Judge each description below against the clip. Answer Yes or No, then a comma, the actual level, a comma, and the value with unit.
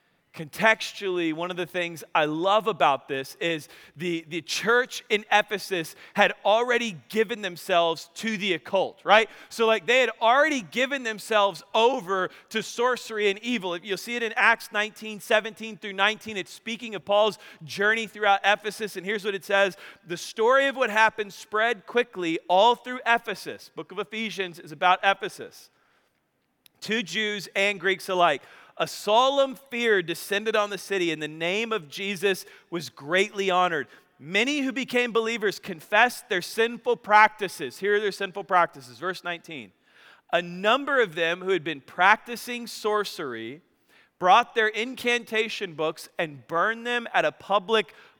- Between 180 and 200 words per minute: No, average, 155 wpm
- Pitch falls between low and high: No, high, 205 Hz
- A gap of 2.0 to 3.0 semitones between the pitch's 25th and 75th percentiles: No, average, 3.8 semitones